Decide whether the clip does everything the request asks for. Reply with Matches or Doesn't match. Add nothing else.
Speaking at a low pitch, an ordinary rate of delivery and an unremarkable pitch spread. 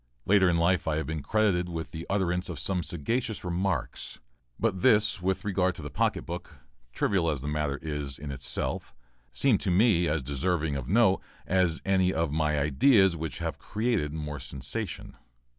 Matches